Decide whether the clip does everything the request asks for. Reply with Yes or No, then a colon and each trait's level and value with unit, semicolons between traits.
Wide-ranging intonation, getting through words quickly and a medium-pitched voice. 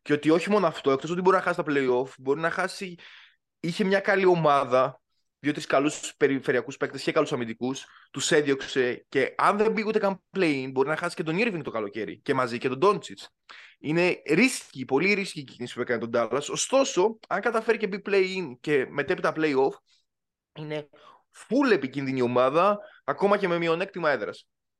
Yes: wide, 6.1 semitones; fast, 185 wpm; medium, 165 Hz